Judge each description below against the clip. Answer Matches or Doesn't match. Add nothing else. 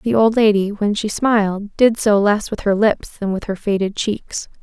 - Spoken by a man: Doesn't match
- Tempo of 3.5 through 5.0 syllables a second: Matches